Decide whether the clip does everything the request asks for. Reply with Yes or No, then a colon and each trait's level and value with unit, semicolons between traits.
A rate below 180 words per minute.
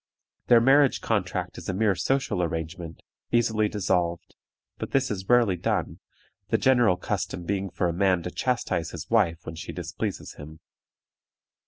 Yes: average, 155 wpm